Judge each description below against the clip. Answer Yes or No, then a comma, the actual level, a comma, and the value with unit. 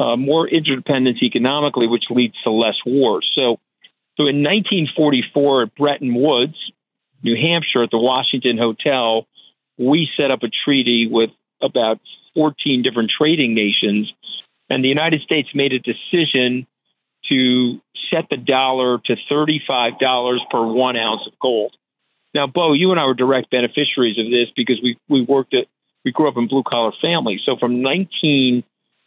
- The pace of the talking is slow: No, average, 165 wpm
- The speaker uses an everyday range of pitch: Yes, average, 3.2 semitones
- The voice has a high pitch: No, low, 130 Hz